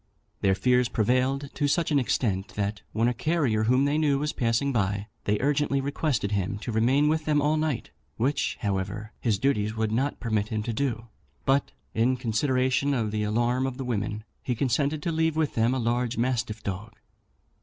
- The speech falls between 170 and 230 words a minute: Yes, average, 190 wpm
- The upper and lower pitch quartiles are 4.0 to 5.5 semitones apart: Yes, average, 4.3 semitones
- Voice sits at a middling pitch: No, low, 125 Hz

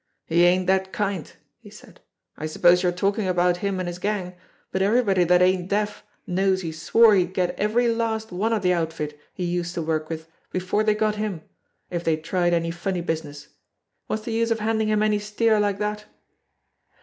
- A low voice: No, medium, 185 Hz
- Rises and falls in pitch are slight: No, average, 3.3 semitones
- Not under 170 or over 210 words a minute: Yes, average, 200 wpm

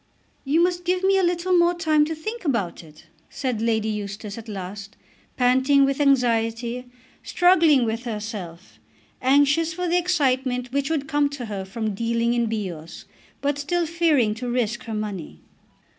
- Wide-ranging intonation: Yes, wide, 6.3 semitones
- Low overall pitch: No, very high, 250 Hz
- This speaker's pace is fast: No, average, 160 wpm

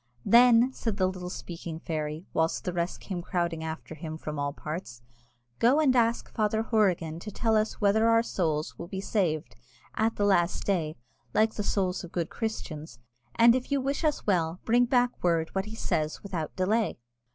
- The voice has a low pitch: No, medium, 185 Hz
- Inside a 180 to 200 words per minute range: Yes, average, 185 wpm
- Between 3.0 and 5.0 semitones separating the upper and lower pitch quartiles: No, wide, 5.6 semitones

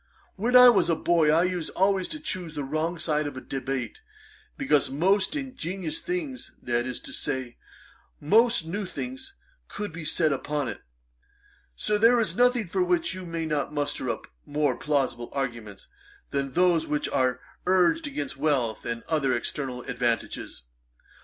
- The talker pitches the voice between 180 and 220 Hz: No, medium, 160 Hz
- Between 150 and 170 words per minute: Yes, average, 160 wpm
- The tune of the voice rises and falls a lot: Yes, wide, 6.6 semitones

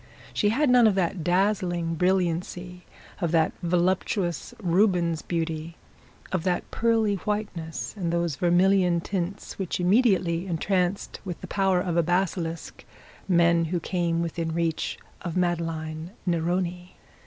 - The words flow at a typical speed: No, slow, 130 wpm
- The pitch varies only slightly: Yes, narrow, 2.1 semitones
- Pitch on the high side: No, medium, 175 Hz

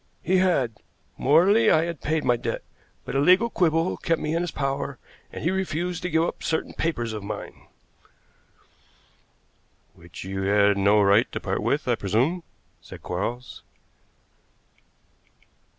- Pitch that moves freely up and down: Yes, wide, 8.2 semitones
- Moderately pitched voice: Yes, medium, 150 Hz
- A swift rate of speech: No, average, 150 wpm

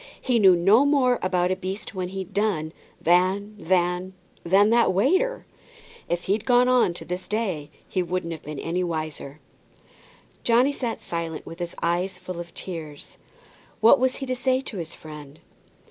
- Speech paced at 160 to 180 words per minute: Yes, average, 170 wpm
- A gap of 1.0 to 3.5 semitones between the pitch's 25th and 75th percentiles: No, average, 4.9 semitones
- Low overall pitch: No, medium, 185 Hz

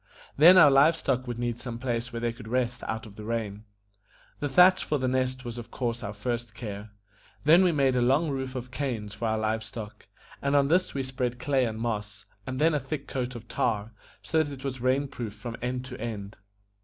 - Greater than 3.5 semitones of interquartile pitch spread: No, average, 3.0 semitones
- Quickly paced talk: Yes, fast, 230 wpm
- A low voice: Yes, low, 125 Hz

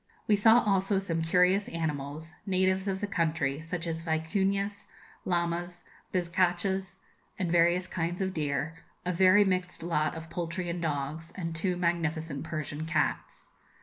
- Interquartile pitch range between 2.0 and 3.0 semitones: Yes, narrow, 2.6 semitones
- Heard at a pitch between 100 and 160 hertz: No, medium, 175 Hz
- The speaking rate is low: No, average, 145 wpm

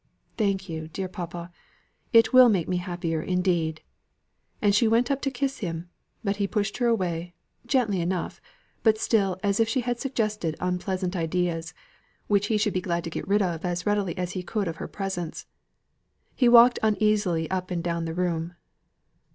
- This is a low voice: No, medium, 185 Hz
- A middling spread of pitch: Yes, average, 3.7 semitones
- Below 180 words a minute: No, average, 185 wpm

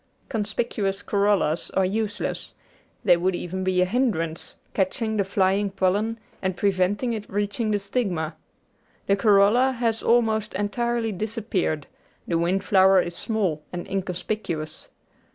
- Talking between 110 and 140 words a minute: Yes, slow, 135 wpm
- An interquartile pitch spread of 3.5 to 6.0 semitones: No, average, 2.9 semitones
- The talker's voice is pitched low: No, high, 200 Hz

